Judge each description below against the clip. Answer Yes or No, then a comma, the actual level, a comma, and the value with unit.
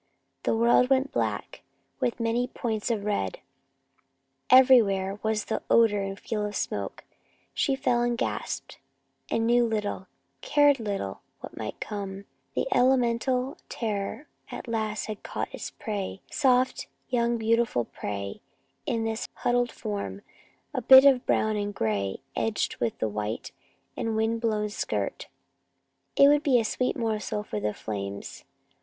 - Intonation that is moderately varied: Yes, average, 3.6 semitones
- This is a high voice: Yes, high, 225 Hz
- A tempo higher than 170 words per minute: No, average, 140 wpm